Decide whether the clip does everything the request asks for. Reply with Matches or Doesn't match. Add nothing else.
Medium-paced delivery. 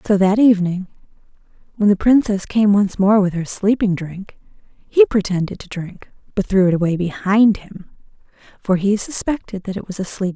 Matches